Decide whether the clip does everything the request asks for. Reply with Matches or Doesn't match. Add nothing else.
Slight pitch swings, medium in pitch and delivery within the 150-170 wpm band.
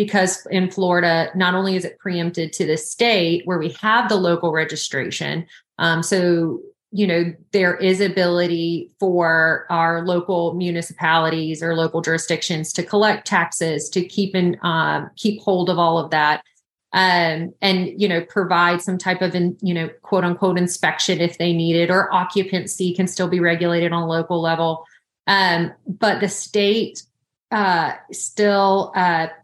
Matches